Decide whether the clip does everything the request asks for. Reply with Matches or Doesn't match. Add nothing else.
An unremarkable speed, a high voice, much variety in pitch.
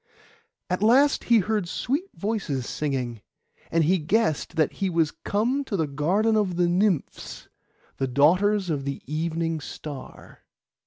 Doesn't match